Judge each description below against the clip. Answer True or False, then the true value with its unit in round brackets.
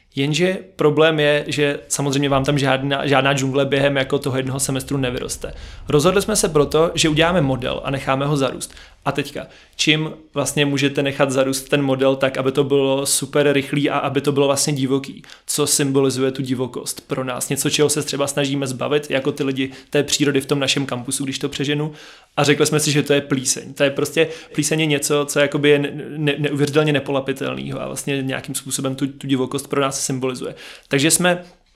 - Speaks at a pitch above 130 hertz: True (140 Hz)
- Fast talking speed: True (195 wpm)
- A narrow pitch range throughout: True (1.5 semitones)